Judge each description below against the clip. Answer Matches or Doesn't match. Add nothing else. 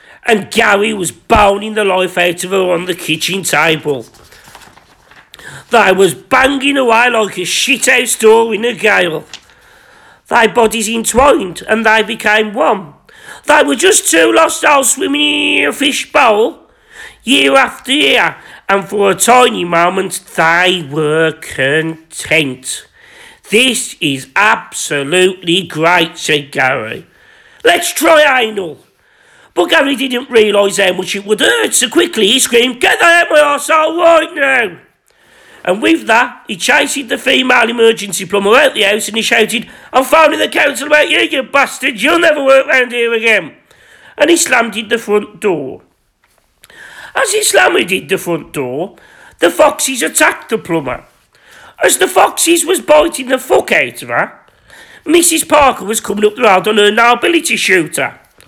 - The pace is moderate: Matches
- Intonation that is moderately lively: Doesn't match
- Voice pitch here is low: Doesn't match